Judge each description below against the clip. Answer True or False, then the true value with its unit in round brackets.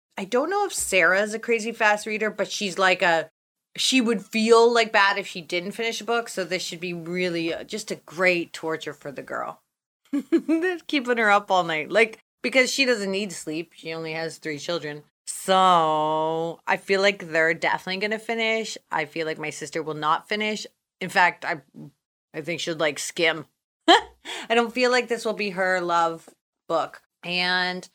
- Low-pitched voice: False (185 Hz)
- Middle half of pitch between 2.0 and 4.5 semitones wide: False (5.3 semitones)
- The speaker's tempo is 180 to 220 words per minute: True (190 wpm)